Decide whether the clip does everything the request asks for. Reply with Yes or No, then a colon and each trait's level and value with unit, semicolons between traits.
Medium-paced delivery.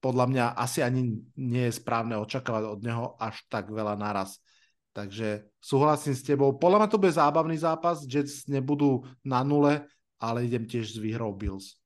No: fast, 170 wpm